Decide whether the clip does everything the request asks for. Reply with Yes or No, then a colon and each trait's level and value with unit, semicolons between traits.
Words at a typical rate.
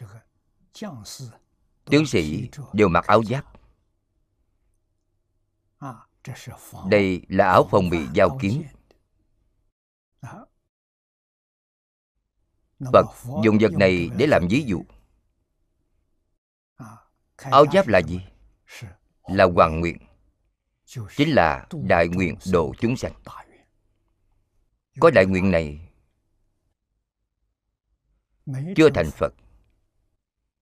No: slow, 80 wpm